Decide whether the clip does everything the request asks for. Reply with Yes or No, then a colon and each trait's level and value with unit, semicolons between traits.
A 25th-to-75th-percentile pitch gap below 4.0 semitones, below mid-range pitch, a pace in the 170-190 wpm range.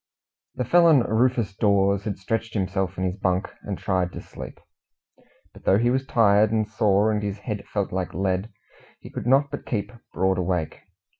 Yes: average, 3.0 semitones; low, 100 Hz; average, 180 wpm